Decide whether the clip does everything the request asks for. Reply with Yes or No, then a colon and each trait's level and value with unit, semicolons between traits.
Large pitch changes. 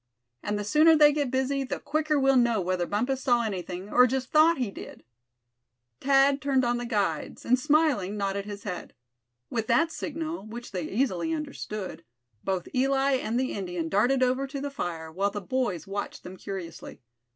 Yes: wide, 5.7 semitones